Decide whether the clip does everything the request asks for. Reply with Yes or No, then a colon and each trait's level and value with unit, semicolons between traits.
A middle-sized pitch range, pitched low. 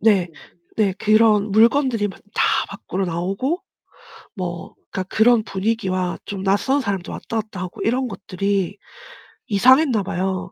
No: average, 3.2 semitones; high, 200 Hz